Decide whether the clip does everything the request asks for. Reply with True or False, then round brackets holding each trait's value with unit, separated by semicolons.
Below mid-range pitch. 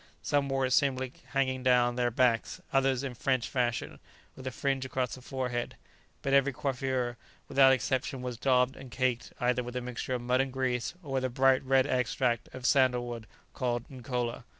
True (130 Hz)